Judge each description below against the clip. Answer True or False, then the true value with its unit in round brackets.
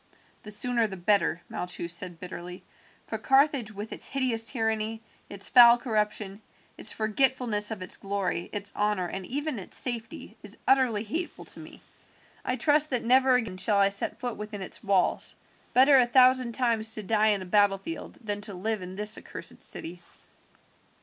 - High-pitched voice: True (215 Hz)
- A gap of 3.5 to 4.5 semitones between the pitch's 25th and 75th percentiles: True (3.8 semitones)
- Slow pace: False (170 wpm)